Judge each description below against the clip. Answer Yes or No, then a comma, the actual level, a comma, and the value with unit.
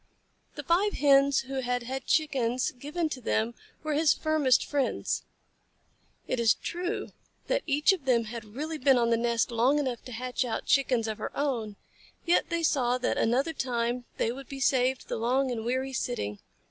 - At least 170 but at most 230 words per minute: Yes, average, 185 wpm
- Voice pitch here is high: Yes, very high, 260 Hz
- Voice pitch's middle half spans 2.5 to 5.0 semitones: Yes, average, 3.3 semitones